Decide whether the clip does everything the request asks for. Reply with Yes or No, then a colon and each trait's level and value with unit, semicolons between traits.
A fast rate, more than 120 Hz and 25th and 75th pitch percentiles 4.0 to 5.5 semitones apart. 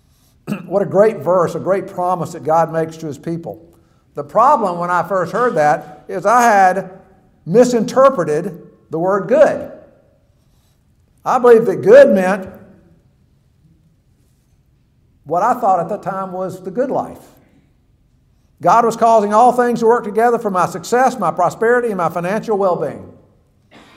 No: average, 150 wpm; high, 190 Hz; average, 4.7 semitones